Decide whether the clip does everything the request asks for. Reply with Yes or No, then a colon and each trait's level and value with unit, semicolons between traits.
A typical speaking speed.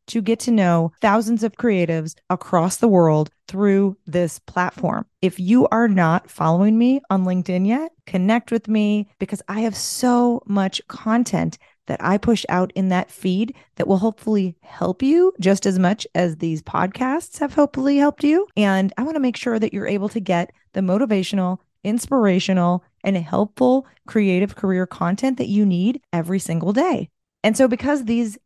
Yes: average, 175 wpm